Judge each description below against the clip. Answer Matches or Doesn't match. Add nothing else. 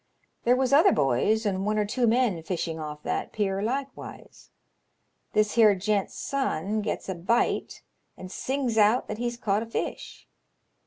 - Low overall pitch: Doesn't match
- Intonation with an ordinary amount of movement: Matches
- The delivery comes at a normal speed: Matches